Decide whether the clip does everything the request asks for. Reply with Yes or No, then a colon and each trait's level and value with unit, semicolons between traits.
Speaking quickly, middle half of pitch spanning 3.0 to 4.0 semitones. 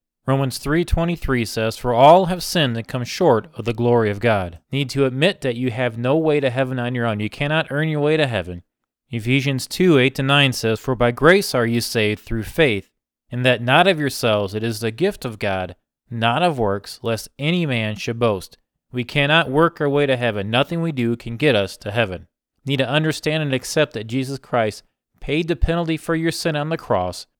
No: fast, 210 wpm; average, 4.8 semitones